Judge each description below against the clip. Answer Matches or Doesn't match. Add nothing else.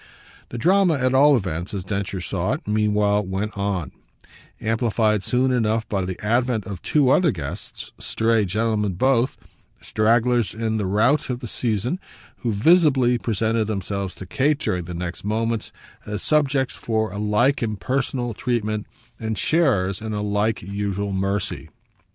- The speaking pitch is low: Matches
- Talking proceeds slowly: Doesn't match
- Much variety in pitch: Doesn't match